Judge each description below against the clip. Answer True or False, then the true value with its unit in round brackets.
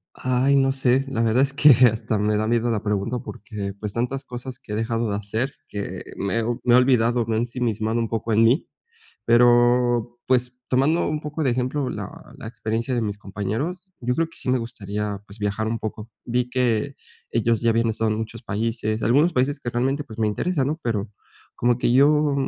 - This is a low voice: True (120 Hz)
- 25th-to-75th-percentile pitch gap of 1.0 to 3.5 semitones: True (2.9 semitones)